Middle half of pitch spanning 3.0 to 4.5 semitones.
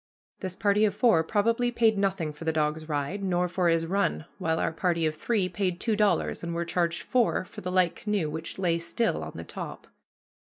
Yes: average, 3.7 semitones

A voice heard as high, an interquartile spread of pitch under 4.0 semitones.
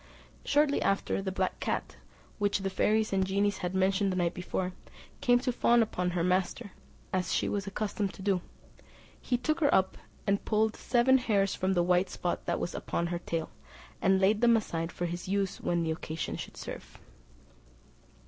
Yes: high, 195 Hz; average, 3.1 semitones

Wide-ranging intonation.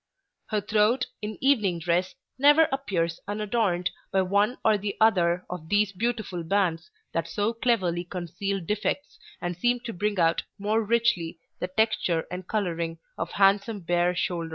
No: average, 3.9 semitones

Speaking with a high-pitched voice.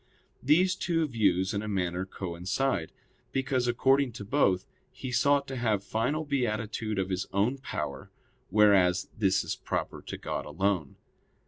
No: low, 110 Hz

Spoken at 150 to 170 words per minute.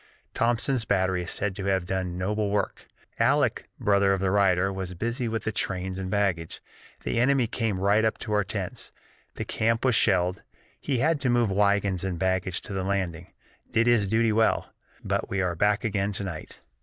No: average, 195 wpm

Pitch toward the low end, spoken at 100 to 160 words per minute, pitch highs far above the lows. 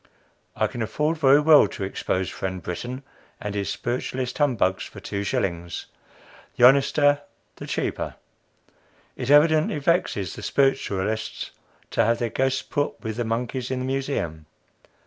Yes: low, 125 Hz; average, 145 wpm; wide, 5.7 semitones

